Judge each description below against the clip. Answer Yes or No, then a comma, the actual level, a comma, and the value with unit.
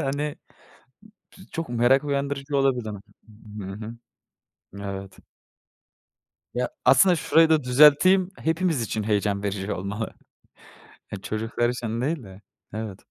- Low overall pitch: Yes, low, 125 Hz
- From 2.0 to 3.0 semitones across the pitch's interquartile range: No, wide, 5.5 semitones